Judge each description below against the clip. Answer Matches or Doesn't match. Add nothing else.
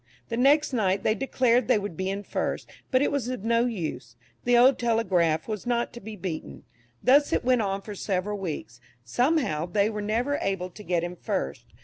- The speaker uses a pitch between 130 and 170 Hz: Doesn't match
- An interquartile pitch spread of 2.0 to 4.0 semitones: Doesn't match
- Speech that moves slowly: Doesn't match